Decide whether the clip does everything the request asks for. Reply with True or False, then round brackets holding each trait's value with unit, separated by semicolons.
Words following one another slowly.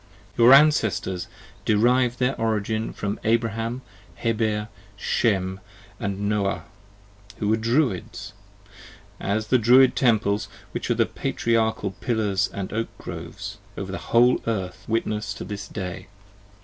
True (130 wpm)